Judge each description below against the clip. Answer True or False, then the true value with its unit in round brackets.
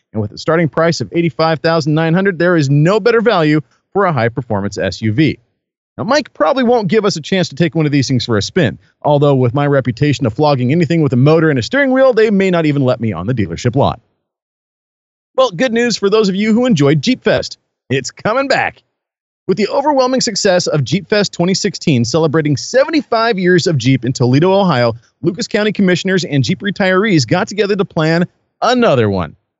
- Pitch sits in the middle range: True (170 Hz)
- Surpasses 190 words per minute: True (205 wpm)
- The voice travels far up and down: True (6.6 semitones)